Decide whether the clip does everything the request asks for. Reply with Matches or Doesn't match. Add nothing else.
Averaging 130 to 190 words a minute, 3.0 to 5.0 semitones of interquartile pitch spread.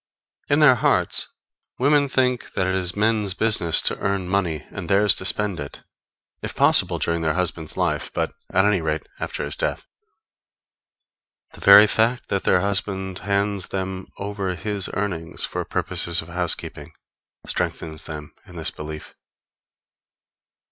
Matches